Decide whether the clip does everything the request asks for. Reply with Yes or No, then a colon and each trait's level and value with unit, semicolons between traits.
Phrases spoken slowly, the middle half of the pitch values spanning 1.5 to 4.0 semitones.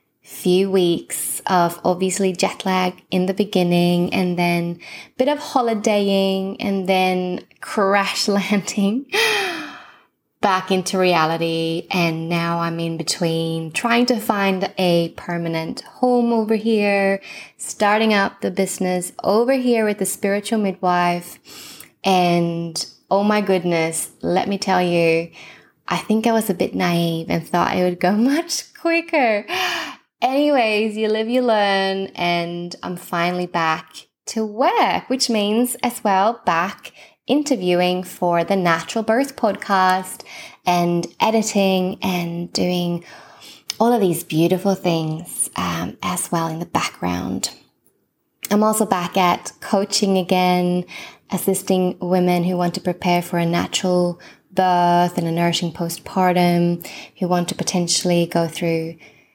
Yes: slow, 130 wpm; average, 3.4 semitones